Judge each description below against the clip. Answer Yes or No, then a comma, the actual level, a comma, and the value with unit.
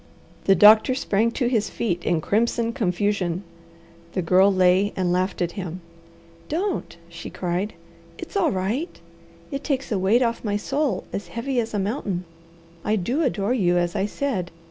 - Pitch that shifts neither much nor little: Yes, average, 4.7 semitones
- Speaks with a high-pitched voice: Yes, high, 205 Hz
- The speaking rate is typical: Yes, average, 165 wpm